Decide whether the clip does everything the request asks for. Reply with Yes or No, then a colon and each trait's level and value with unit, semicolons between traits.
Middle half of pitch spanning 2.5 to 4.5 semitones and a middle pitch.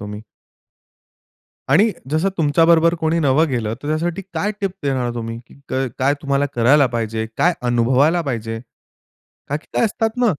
No: wide, 5.6 semitones; medium, 145 Hz